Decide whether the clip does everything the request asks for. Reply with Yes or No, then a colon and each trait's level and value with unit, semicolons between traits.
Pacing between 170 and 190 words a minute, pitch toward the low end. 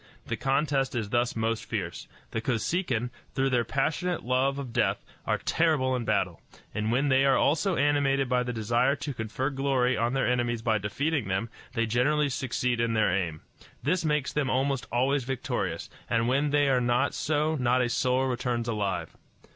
Yes: average, 180 wpm; low, 125 Hz